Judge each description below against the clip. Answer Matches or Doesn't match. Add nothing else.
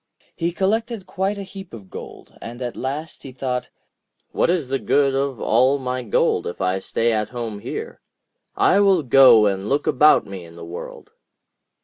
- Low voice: Matches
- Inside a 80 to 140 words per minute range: Doesn't match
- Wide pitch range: Matches